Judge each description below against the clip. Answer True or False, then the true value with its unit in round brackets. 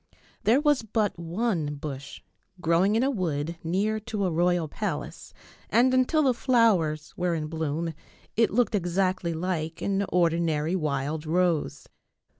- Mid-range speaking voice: True (175 Hz)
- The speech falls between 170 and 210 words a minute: False (140 wpm)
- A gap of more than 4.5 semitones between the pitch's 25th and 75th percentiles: True (5.2 semitones)